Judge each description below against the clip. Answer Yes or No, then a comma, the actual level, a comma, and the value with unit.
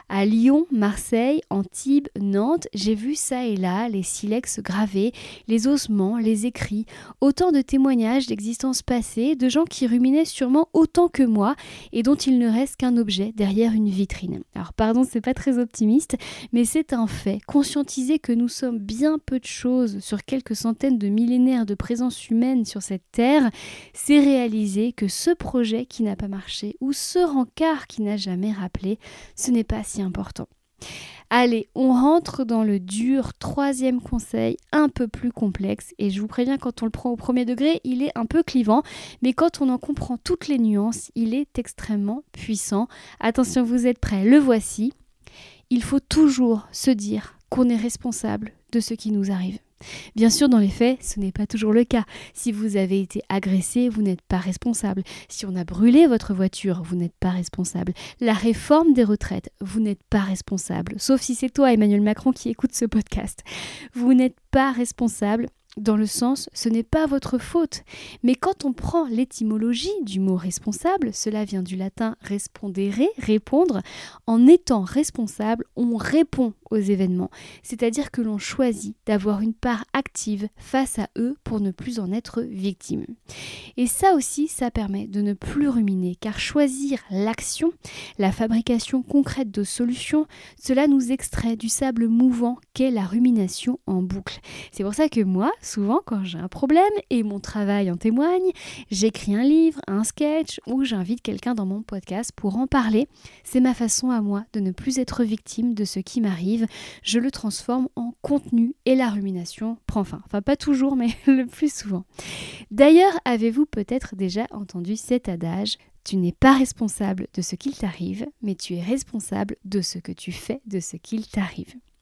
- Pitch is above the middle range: Yes, high, 230 Hz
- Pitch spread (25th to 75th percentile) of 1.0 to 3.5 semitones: No, average, 4.1 semitones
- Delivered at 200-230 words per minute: No, average, 180 wpm